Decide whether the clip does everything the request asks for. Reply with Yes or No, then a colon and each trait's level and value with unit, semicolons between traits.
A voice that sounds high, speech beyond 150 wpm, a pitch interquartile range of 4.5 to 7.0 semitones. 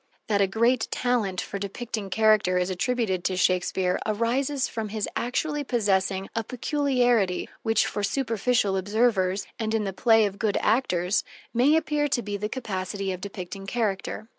No: high, 215 Hz; average, 160 wpm; average, 4.0 semitones